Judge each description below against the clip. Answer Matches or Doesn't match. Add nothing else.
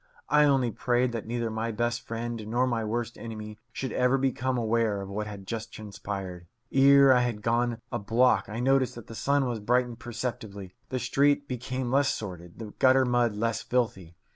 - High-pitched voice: Doesn't match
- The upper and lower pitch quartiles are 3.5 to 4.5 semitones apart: Doesn't match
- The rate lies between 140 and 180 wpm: Doesn't match